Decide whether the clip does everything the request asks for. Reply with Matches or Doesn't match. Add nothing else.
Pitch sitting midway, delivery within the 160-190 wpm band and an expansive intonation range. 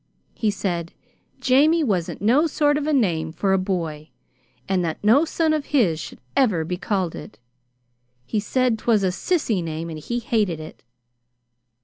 Doesn't match